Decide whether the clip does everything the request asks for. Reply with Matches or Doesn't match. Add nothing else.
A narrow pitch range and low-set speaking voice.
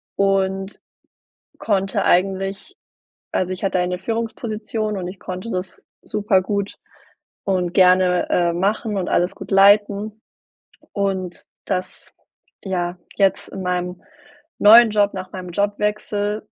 Doesn't match